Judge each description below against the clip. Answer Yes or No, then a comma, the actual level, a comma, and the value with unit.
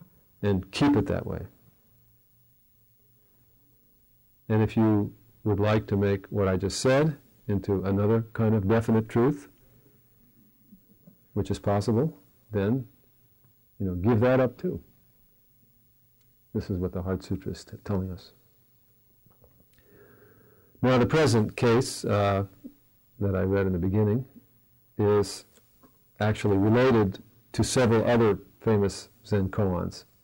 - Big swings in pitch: No, average, 2.9 semitones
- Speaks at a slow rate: Yes, slow, 125 wpm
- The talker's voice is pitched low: Yes, low, 110 Hz